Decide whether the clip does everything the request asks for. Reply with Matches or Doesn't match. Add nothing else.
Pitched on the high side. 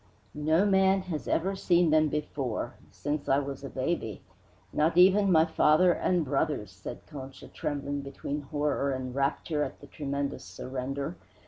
Doesn't match